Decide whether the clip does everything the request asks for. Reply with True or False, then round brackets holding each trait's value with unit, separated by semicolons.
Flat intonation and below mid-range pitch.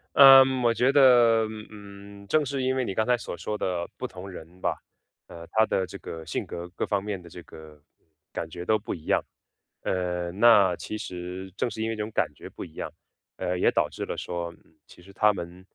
False (4.2 semitones; 100 Hz)